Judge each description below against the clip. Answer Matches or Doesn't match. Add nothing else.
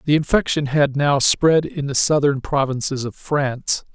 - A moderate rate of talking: Matches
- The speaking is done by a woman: Doesn't match